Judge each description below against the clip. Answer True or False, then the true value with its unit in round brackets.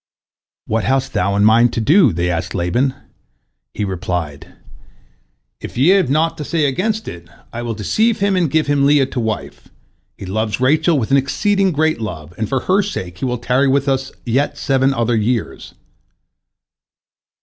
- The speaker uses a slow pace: False (175 wpm)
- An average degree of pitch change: False (6.1 semitones)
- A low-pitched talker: True (130 Hz)